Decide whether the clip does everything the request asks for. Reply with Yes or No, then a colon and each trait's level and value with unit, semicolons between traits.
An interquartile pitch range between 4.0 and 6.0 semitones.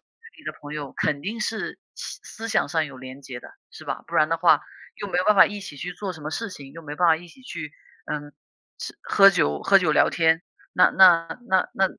Yes: average, 4.7 semitones